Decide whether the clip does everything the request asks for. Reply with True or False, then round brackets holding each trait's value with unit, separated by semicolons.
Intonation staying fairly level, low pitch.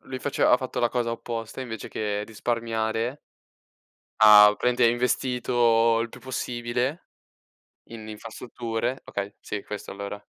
True (2.1 semitones; 115 Hz)